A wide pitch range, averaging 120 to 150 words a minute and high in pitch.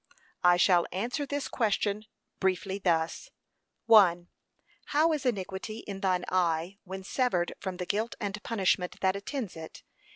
No: average, 3.6 semitones; average, 140 wpm; high, 195 Hz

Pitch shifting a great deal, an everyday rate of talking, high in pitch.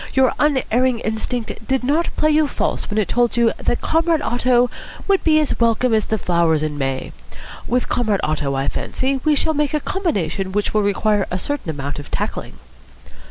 Yes: wide, 6.7 semitones; average, 190 wpm; high, 235 Hz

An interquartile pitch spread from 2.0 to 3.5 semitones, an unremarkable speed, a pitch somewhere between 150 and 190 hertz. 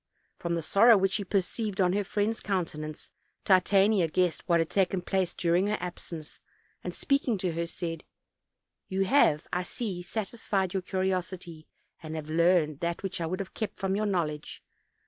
Yes: average, 2.7 semitones; average, 170 wpm; medium, 185 Hz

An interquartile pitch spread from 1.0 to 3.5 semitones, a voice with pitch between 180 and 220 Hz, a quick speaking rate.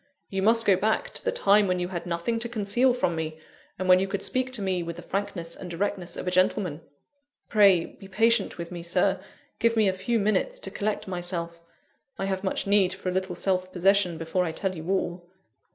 Yes: average, 2.7 semitones; high, 190 Hz; fast, 220 wpm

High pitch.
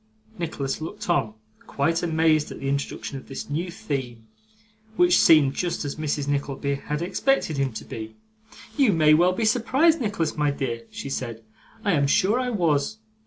No: medium, 155 Hz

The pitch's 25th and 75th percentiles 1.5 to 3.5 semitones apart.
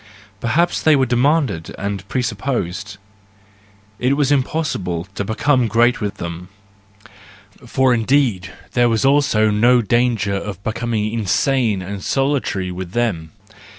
No: average, 4.9 semitones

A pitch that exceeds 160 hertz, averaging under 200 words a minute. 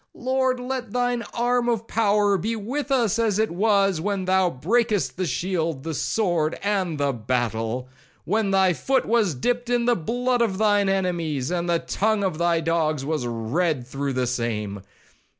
Yes: high, 190 Hz; average, 170 wpm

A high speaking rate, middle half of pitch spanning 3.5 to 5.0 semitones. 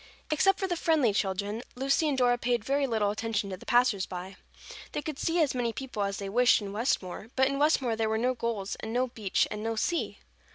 Yes: fast, 230 wpm; average, 4.4 semitones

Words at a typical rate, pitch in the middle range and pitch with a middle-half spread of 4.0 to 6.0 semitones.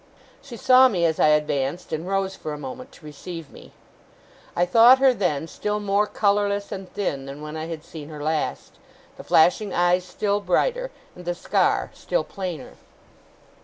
Yes: average, 175 wpm; medium, 180 Hz; average, 4.9 semitones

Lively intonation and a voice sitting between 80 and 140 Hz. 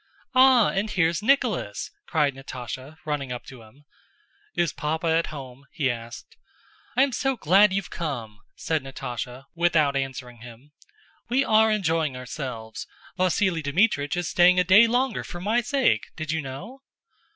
No: wide, 7.0 semitones; medium, 160 Hz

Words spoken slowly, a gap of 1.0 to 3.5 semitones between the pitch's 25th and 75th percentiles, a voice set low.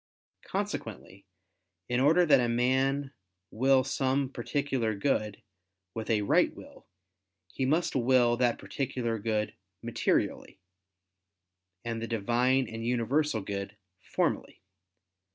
Yes: slow, 110 wpm; average, 3.0 semitones; low, 120 Hz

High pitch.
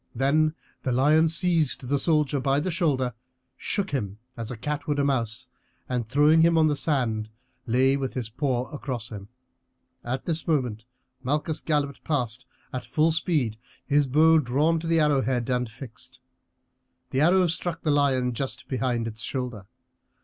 No: low, 135 Hz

